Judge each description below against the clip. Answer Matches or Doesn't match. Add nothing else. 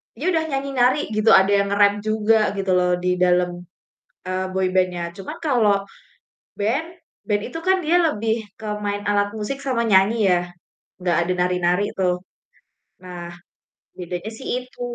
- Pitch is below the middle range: Doesn't match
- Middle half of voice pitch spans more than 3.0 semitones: Matches